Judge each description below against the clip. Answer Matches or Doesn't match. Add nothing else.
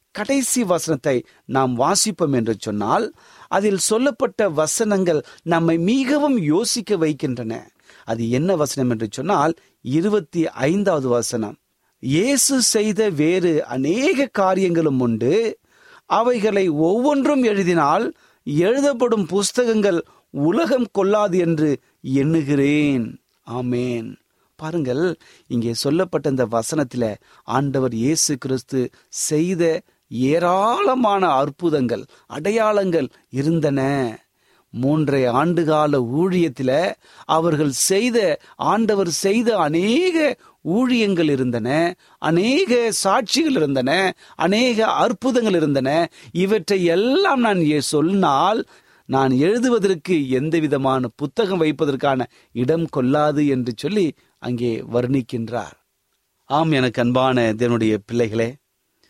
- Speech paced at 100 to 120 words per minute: Doesn't match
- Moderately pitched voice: Matches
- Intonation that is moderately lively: Doesn't match